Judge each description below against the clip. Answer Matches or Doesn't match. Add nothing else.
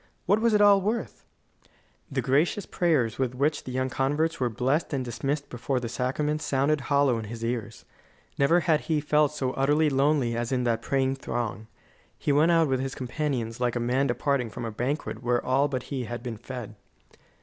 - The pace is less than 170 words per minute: Doesn't match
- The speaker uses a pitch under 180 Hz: Matches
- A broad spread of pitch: Doesn't match